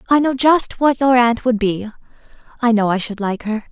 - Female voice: Yes, female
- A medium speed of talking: No, fast, 225 wpm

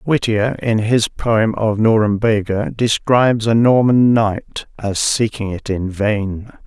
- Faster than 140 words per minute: No, slow, 135 wpm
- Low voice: Yes, low, 110 Hz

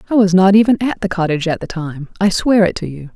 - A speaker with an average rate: No, fast, 285 wpm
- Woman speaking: Yes, female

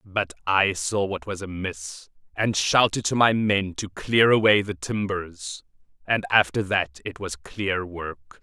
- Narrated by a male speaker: Yes, male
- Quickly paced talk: No, average, 165 wpm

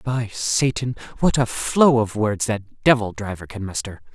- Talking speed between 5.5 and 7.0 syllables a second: No, 4.4 syllables/s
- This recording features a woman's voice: No, male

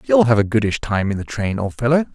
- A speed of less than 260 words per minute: No, fast, 280 wpm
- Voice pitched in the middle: No, low, 115 Hz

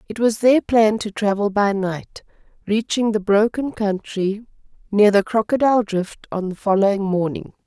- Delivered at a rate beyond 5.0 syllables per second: No, 4.6 syllables/s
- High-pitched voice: Yes, high, 210 Hz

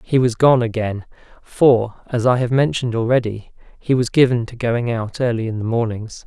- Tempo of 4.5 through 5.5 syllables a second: Yes, 5.1 syllables/s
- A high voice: No, low, 120 Hz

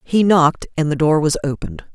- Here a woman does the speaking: Yes, female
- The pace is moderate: No, fast, 215 wpm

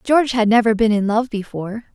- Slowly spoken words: No, fast, 215 wpm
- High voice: Yes, high, 225 Hz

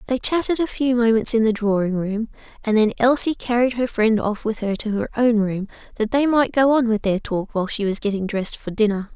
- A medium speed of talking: No, fast, 245 wpm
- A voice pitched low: No, high, 225 Hz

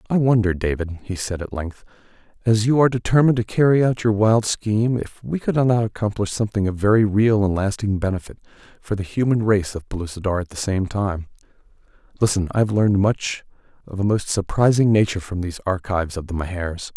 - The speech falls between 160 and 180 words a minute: No, average, 195 wpm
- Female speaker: No, male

